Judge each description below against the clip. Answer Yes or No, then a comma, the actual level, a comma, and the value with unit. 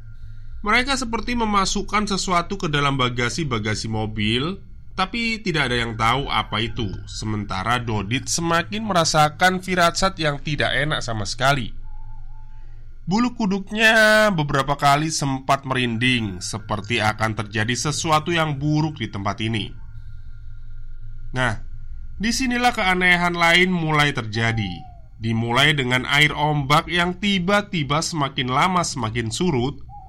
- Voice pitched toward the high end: No, low, 135 Hz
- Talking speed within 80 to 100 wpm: No, average, 110 wpm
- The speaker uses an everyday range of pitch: No, wide, 7.8 semitones